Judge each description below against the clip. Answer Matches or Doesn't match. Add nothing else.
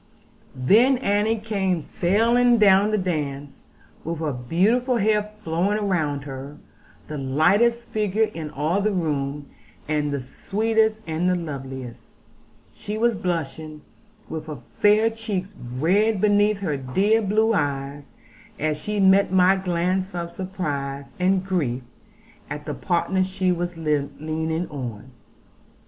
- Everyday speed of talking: Doesn't match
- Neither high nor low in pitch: Matches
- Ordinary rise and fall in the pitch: Doesn't match